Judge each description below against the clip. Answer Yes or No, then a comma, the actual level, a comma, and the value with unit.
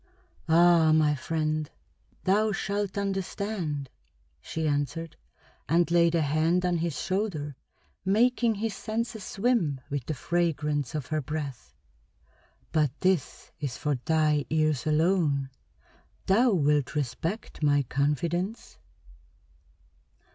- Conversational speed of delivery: No, slow, 110 wpm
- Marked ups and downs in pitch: No, average, 4.4 semitones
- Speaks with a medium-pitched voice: Yes, medium, 160 Hz